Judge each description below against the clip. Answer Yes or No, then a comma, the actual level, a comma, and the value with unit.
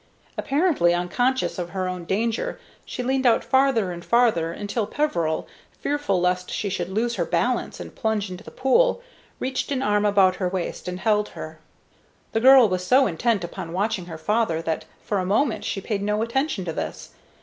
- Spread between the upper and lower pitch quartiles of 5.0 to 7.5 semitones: Yes, average, 5.3 semitones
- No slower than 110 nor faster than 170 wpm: No, average, 185 wpm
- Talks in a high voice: Yes, high, 205 Hz